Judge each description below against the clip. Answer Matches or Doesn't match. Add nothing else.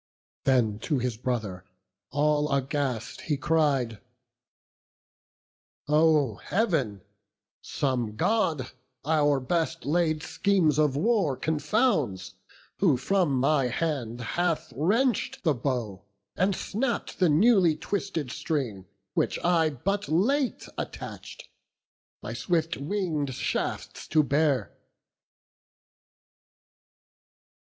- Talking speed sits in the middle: Doesn't match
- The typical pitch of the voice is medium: Matches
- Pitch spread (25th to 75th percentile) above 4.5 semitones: Matches